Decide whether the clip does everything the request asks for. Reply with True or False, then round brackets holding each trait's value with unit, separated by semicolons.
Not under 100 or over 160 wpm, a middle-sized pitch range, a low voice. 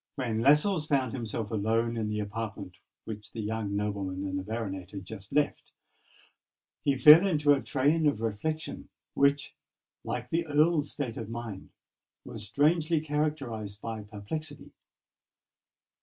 False (140 wpm; 5.9 semitones; 115 Hz)